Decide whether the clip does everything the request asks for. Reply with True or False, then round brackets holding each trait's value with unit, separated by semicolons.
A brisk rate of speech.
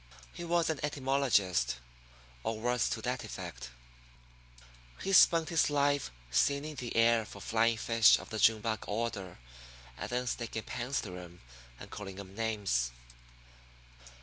False (145 wpm)